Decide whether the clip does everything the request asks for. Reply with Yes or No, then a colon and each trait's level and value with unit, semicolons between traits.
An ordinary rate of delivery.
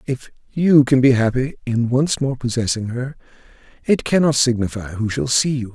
Yes: average, 180 wpm